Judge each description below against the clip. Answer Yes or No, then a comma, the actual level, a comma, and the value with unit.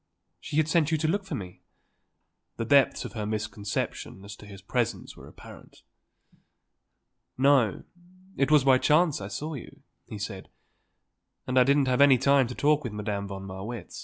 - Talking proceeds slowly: No, average, 165 wpm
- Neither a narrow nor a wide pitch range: No, wide, 5.7 semitones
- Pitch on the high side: No, low, 125 Hz